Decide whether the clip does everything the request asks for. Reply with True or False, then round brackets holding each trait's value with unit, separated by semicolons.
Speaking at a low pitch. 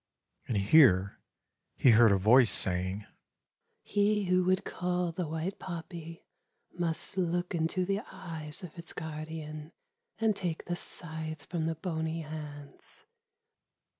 False (160 Hz)